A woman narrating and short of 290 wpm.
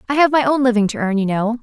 No: female; fast, 335 wpm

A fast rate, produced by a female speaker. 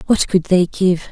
Yes: fast, 215 wpm; female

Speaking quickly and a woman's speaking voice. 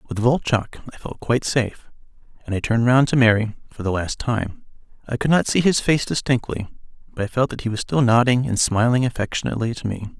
No: fast, 210 wpm; male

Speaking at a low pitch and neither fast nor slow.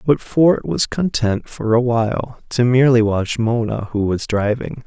Yes: low, 120 Hz; average, 175 wpm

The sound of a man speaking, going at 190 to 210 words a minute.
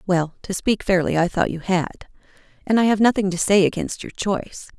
No: female; average, 200 wpm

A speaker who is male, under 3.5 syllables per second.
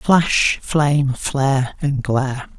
Yes: male; 3.3 syllables/s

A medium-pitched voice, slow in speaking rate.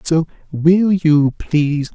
Yes: medium, 160 Hz; slow, 125 wpm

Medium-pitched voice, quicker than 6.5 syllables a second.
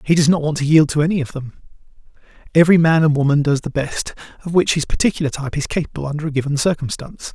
Yes: medium, 150 Hz; 7.3 syllables/s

